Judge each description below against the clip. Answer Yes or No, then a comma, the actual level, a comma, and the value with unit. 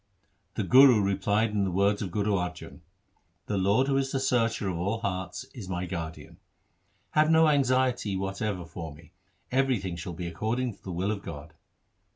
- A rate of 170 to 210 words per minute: Yes, average, 190 wpm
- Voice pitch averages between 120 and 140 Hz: No, low, 100 Hz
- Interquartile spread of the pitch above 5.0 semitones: Yes, wide, 5.4 semitones